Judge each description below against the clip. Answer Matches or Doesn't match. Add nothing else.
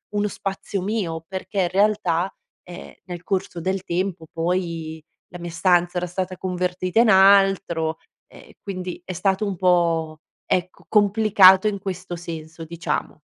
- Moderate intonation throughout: Doesn't match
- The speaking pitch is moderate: Matches